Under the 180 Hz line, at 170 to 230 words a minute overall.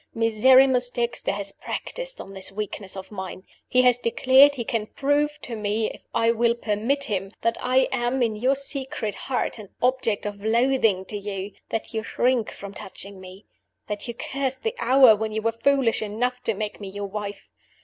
No: high, 230 Hz; average, 190 wpm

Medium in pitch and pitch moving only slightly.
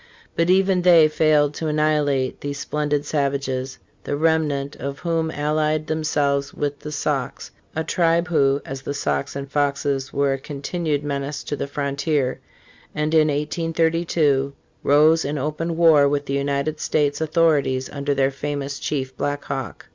Yes: medium, 145 Hz; narrow, 2.0 semitones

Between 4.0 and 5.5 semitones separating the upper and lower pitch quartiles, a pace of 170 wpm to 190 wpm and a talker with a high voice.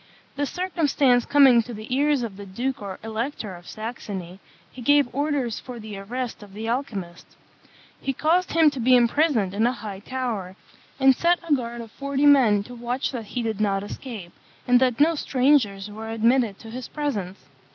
Yes: average, 4.5 semitones; average, 185 wpm; high, 240 Hz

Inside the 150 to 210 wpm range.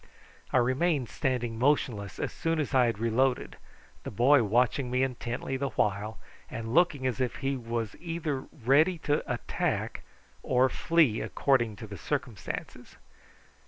No: average, 140 wpm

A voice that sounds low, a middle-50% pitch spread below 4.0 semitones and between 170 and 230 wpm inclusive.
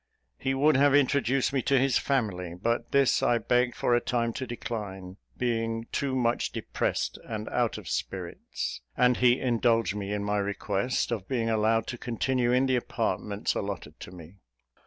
Yes: low, 115 Hz; average, 3.6 semitones; average, 175 wpm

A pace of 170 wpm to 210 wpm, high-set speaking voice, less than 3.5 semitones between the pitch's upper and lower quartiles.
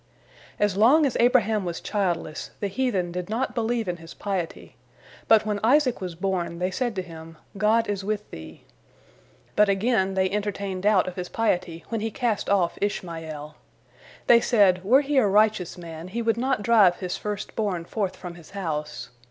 No: average, 180 wpm; high, 200 Hz; average, 4.0 semitones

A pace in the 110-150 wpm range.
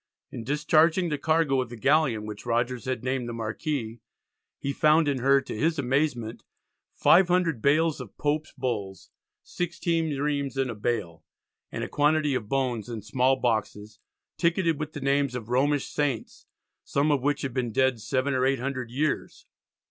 No: average, 165 wpm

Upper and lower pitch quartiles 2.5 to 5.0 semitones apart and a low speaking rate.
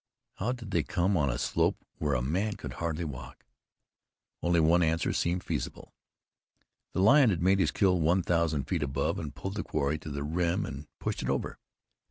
No: average, 3.9 semitones; average, 195 wpm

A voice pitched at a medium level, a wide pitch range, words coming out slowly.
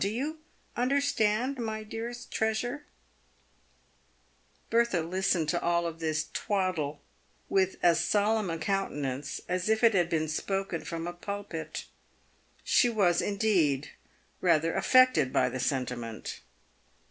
Yes: medium, 180 Hz; wide, 5.8 semitones; slow, 125 wpm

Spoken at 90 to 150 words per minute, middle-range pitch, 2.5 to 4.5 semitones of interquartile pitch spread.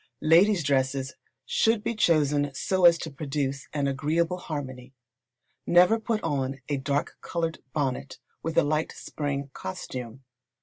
Yes: slow, 135 wpm; medium, 145 Hz; average, 3.7 semitones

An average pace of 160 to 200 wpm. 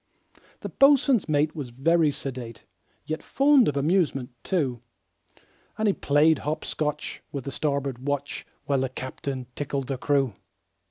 No: average, 145 wpm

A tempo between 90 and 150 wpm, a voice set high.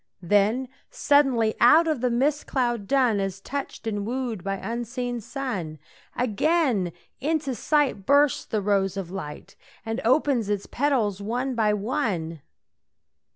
Yes: slow, 135 wpm; high, 235 Hz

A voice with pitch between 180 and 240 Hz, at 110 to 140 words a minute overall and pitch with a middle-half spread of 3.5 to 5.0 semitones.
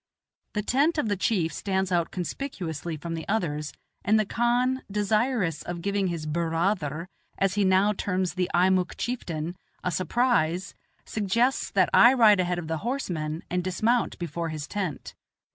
No: medium, 185 Hz; average, 165 wpm; average, 4.4 semitones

